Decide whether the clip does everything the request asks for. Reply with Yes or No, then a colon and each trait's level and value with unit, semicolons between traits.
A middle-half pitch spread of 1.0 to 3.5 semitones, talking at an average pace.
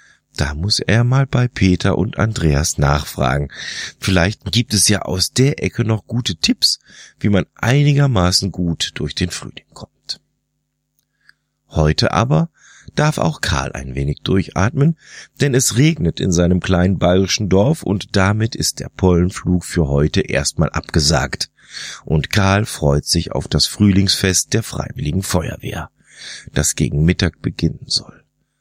No: average, 4.7 semitones; average, 140 wpm